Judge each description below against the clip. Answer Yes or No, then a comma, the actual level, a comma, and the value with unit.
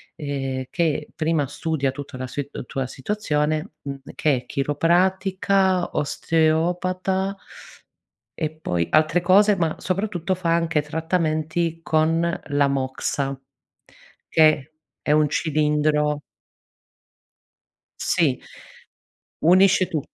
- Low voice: No, medium, 155 Hz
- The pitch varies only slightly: No, average, 3.4 semitones